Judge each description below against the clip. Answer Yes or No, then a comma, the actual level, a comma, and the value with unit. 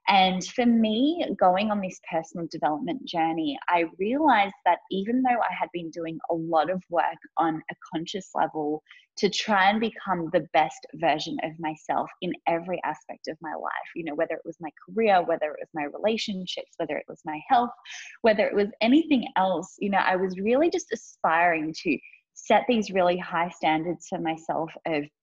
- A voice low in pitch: No, medium, 185 Hz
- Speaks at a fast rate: No, average, 190 wpm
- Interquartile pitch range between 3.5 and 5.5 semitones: Yes, average, 4.8 semitones